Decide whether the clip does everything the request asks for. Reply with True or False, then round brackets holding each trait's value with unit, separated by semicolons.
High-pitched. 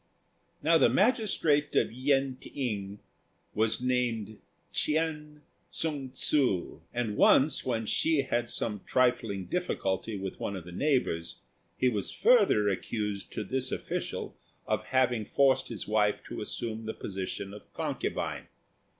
False (120 Hz)